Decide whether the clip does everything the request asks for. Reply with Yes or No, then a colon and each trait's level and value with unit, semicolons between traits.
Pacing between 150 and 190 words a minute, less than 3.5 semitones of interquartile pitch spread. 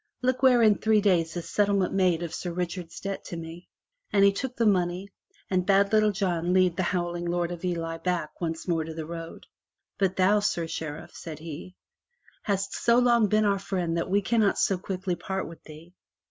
No: average, 200 wpm; average, 2.9 semitones